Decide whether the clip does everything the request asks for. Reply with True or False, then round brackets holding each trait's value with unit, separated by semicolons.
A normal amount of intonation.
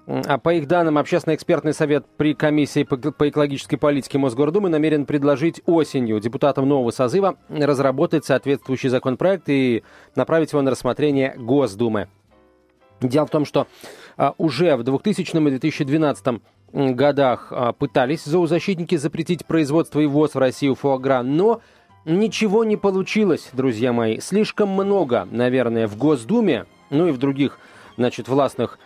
True (3.9 semitones)